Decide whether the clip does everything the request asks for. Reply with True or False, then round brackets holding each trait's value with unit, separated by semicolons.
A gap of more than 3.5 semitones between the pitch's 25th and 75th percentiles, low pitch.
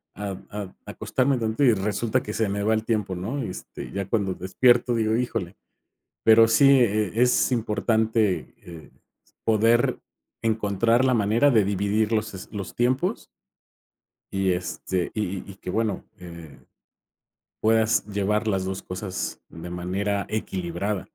False (3.0 semitones; 105 Hz)